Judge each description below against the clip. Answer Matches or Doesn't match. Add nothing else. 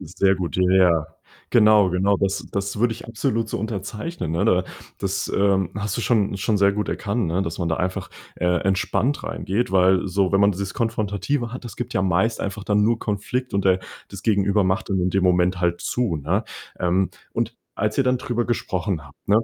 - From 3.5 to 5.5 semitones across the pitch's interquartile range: Doesn't match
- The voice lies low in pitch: Matches